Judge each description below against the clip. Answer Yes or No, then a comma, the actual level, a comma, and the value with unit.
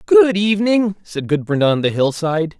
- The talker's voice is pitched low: No, medium, 180 Hz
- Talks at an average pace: Yes, average, 185 wpm